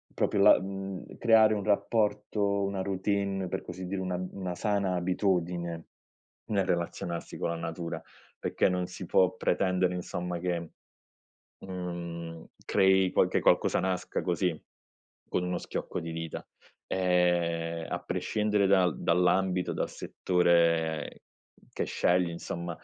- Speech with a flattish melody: Yes, narrow, 2.1 semitones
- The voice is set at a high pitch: No, very low, 90 Hz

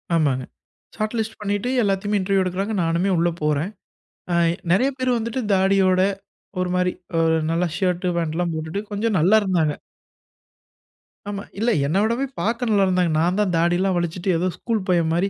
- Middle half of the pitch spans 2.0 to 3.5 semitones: Yes, average, 3.1 semitones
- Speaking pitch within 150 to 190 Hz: Yes, medium, 185 Hz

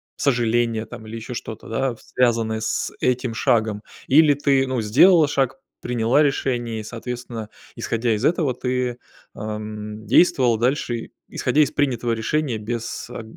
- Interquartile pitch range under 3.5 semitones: Yes, average, 3.1 semitones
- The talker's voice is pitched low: Yes, low, 120 Hz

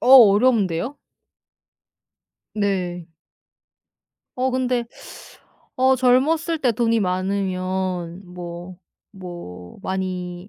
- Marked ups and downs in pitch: Yes, wide, 5.7 semitones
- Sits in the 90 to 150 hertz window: No, high, 190 Hz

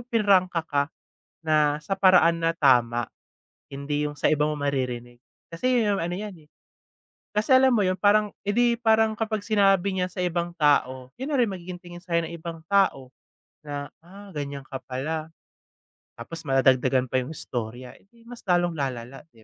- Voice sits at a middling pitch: Yes, medium, 165 Hz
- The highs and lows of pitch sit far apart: Yes, wide, 6.3 semitones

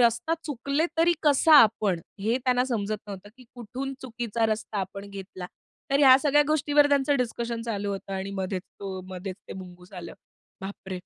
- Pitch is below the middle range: No, high, 225 Hz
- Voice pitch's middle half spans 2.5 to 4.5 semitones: No, average, 5.3 semitones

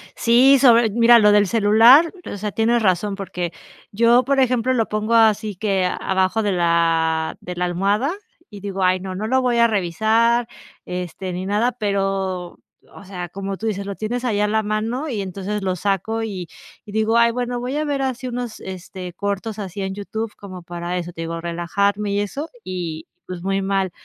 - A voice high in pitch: Yes, high, 205 Hz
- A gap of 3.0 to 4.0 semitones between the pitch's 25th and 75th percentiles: Yes, average, 3.7 semitones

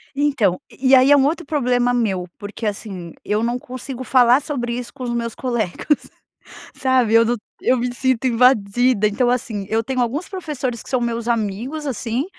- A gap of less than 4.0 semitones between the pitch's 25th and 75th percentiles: Yes, narrow, 2.4 semitones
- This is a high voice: Yes, high, 245 Hz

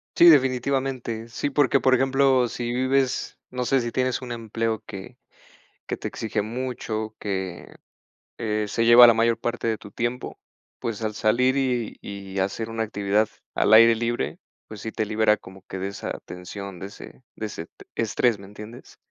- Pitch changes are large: No, average, 3.0 semitones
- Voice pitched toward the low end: Yes, low, 115 Hz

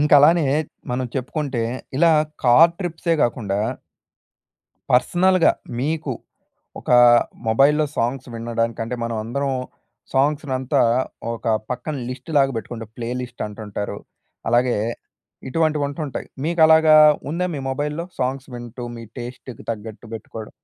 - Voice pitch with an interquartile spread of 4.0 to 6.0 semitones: Yes, average, 4.5 semitones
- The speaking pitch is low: Yes, low, 130 Hz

